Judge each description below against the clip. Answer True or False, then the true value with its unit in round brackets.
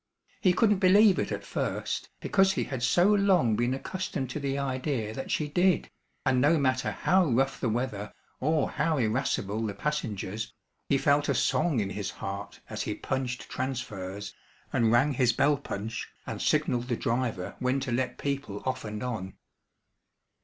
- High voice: False (130 Hz)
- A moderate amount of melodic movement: True (4.8 semitones)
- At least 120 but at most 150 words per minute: False (170 wpm)